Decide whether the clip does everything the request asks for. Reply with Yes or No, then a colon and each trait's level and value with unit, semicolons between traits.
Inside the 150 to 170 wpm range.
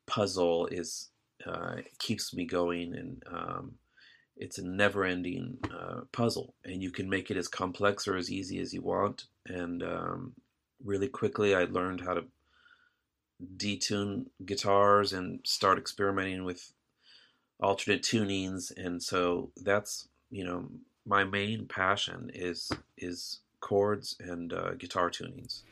No: slow, 135 wpm